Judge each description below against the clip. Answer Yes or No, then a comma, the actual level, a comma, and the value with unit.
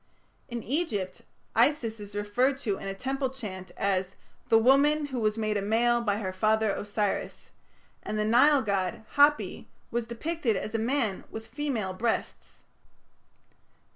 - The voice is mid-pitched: No, high, 225 Hz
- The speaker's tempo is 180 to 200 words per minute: No, average, 150 wpm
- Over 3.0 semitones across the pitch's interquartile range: Yes, average, 4.2 semitones